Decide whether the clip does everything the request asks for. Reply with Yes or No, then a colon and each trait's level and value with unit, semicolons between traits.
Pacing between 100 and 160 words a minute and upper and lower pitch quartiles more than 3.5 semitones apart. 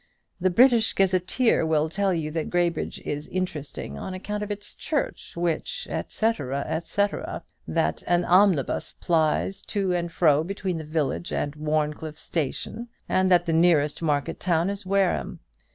Yes: average, 150 wpm; average, 4.0 semitones